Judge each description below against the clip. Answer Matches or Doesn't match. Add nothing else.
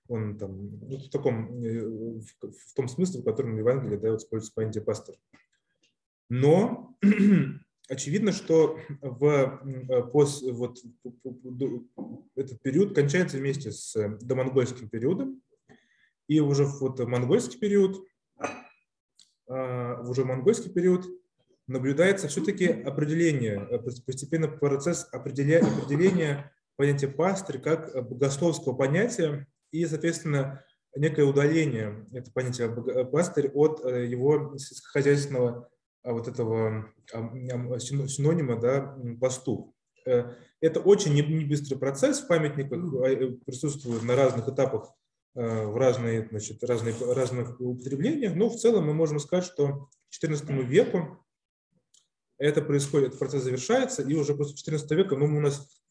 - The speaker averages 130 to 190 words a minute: Doesn't match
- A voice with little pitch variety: Doesn't match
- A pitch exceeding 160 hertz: Doesn't match